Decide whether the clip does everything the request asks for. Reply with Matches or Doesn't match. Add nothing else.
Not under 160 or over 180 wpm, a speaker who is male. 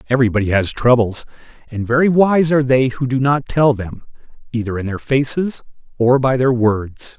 Matches